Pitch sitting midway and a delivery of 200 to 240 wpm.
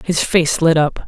Yes: medium, 160 Hz; fast, 225 wpm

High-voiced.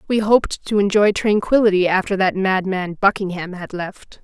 Yes: high, 195 Hz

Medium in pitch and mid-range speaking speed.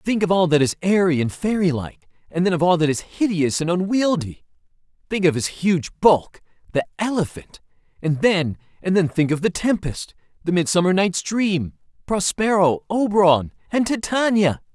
Yes: medium, 180 Hz; average, 155 wpm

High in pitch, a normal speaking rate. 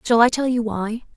No: high, 230 Hz; fast, 260 wpm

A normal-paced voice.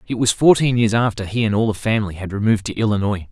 No: fast, 255 wpm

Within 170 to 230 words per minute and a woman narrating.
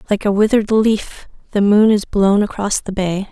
Yes: average, 200 wpm; female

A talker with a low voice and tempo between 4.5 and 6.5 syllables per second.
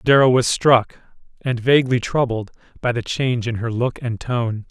Yes: low, 120 Hz; 4.9 syllables/s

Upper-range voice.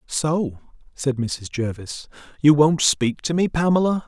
No: medium, 145 Hz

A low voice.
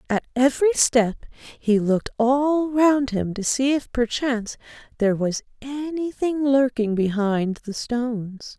No: high, 245 Hz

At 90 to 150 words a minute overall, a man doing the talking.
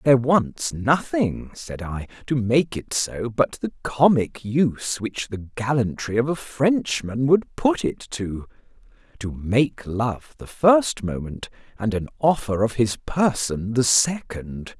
Yes: average, 145 wpm; male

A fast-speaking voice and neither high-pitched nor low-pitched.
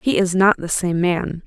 Yes: fast, 245 wpm; medium, 180 Hz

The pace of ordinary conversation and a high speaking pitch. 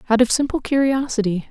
Yes: average, 160 wpm; high, 245 Hz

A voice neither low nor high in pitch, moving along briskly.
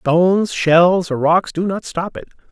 No: medium, 175 Hz; average, 190 wpm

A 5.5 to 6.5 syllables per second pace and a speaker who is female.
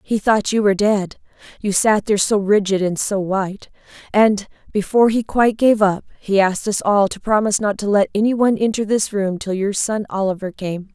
Yes: 5.6 syllables/s; female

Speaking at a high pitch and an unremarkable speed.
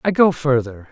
No: medium, 140 Hz; average, 195 wpm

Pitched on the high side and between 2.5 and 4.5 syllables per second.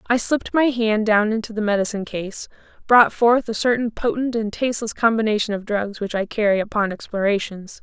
No: high, 220 Hz; 5.6 syllables/s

